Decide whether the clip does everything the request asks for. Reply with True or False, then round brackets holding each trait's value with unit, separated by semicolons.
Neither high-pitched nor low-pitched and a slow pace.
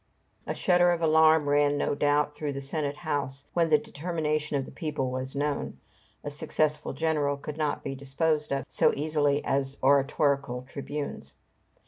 False (145 Hz; 160 wpm)